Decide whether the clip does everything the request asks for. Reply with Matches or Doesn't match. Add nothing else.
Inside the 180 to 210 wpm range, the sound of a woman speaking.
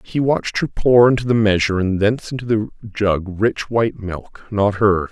Doesn't match